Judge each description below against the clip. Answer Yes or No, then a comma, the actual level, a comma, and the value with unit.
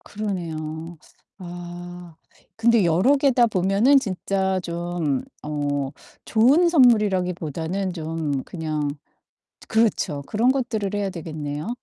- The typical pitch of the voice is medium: Yes, medium, 180 Hz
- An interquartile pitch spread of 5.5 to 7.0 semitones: No, average, 5.1 semitones